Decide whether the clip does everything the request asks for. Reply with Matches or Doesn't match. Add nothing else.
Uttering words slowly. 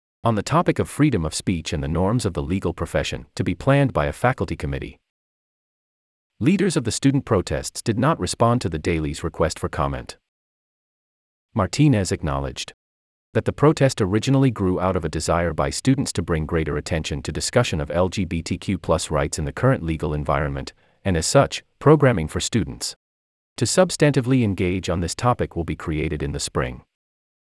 Doesn't match